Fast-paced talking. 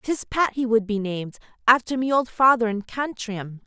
No: average, 195 wpm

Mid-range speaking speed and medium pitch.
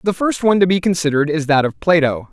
No: fast, 260 wpm; medium, 165 Hz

